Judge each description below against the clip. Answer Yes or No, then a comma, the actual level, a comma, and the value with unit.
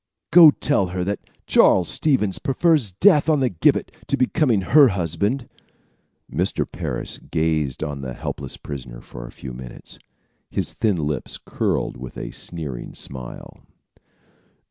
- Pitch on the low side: Yes, very low, 90 Hz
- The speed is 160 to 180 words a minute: No, slow, 135 wpm